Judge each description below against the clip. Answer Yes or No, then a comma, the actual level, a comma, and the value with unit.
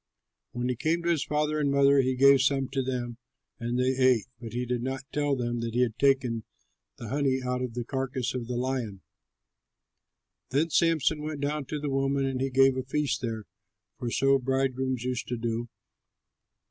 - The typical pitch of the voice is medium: No, low, 130 Hz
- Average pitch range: No, narrow, 2.1 semitones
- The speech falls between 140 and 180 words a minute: No, average, 195 wpm